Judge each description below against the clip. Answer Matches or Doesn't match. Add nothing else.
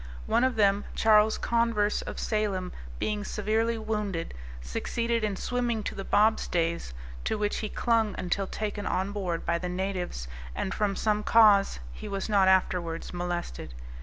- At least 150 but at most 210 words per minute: Matches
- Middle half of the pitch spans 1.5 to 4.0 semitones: Matches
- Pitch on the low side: Doesn't match